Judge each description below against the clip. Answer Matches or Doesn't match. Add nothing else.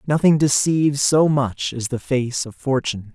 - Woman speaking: Doesn't match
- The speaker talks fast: Doesn't match